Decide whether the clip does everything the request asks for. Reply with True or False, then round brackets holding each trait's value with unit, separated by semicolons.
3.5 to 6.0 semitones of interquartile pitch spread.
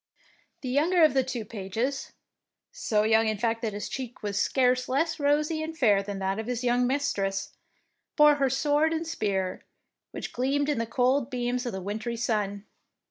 True (5.0 semitones)